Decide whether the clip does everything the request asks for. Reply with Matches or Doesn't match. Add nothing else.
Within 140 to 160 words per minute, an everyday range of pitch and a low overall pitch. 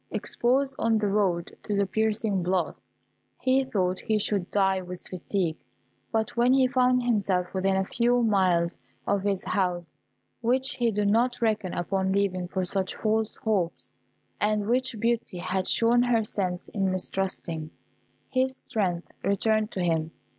Doesn't match